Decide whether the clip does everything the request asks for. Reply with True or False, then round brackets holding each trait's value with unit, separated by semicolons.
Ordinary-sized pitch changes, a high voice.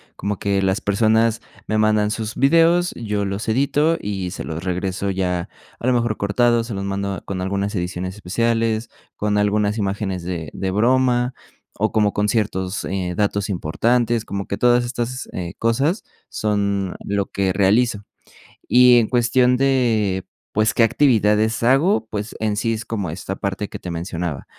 False (3.3 semitones; 105 Hz)